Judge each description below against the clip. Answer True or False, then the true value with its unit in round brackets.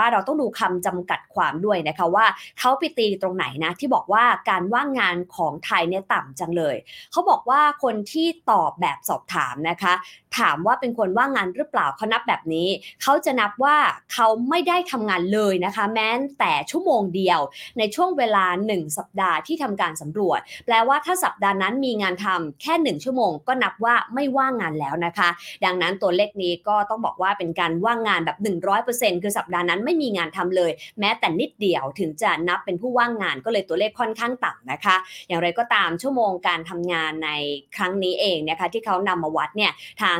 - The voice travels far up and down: True (5.8 semitones)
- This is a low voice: False (205 Hz)